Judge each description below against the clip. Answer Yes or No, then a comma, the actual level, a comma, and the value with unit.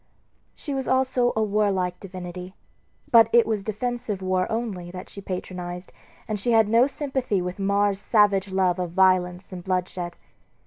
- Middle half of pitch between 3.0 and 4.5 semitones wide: Yes, average, 3.6 semitones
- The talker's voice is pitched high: Yes, high, 195 Hz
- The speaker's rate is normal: Yes, average, 155 wpm